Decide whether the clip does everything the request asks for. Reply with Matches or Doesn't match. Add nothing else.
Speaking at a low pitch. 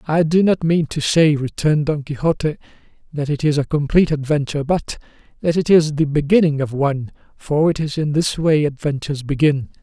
Doesn't match